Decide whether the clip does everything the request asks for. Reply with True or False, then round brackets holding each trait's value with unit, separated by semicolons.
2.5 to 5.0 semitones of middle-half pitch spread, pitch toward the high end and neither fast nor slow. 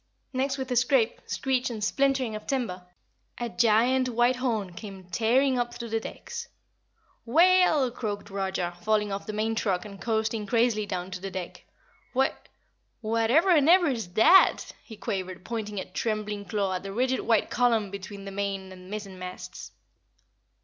True (4.1 semitones; 220 Hz; 165 wpm)